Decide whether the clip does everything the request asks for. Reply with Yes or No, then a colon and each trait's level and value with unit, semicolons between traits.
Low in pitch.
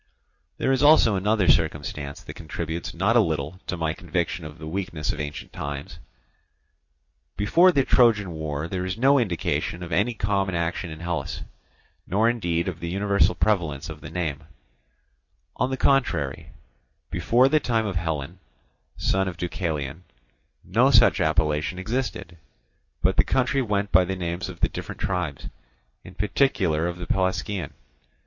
Yes: very low, 90 Hz